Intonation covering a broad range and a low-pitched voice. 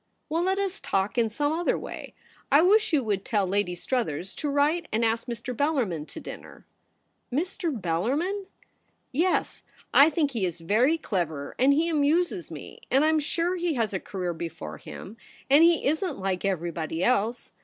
No: wide, 8.8 semitones; very high, 255 Hz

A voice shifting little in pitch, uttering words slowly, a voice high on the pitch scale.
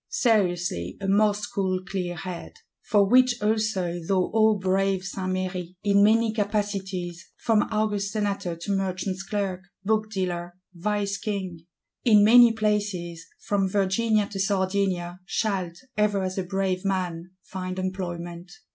Yes: narrow, 2.3 semitones; slow, 130 wpm; high, 195 Hz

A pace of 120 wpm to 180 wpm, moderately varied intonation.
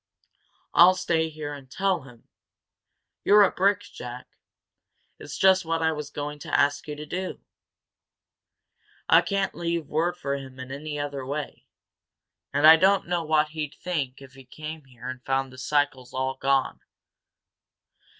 Yes: average, 160 wpm; average, 3.8 semitones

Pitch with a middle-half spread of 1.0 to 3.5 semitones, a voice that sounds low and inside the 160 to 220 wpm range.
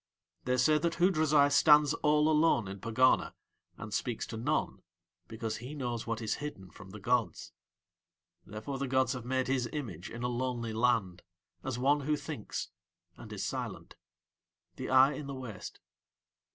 No: average, 4.4 semitones; low, 125 Hz; average, 165 wpm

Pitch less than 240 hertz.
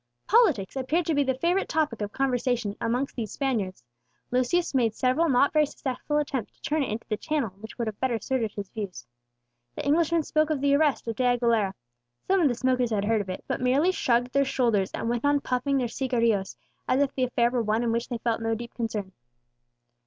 No: very high, 250 Hz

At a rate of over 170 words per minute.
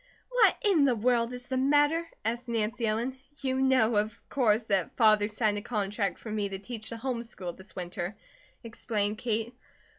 Yes: average, 180 wpm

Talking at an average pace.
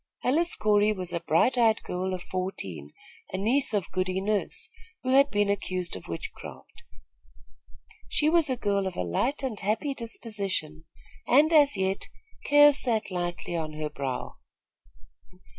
Yes: average, 150 wpm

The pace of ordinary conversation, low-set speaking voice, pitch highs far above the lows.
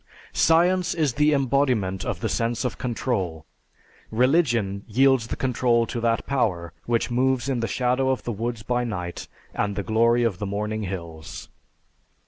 No: average, 160 wpm; low, 120 Hz; average, 4.1 semitones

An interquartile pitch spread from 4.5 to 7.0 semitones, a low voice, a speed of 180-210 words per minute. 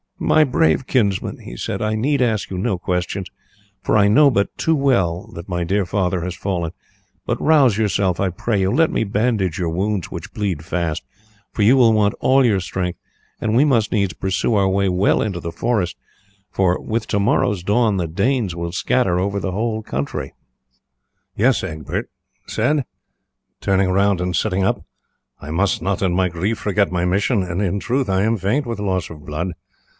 No: average, 3.6 semitones; low, 100 Hz; average, 190 wpm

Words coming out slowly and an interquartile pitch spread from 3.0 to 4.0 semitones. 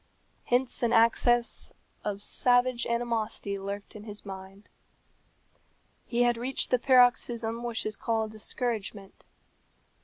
No: slow, 115 wpm; narrow, 2.5 semitones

